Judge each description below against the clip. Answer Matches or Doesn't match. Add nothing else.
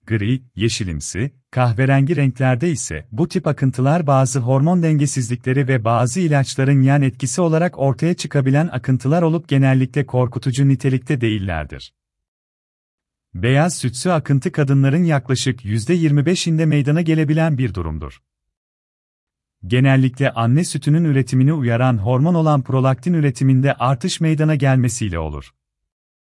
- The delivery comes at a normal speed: Matches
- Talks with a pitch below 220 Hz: Matches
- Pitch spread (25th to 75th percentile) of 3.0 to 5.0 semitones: Matches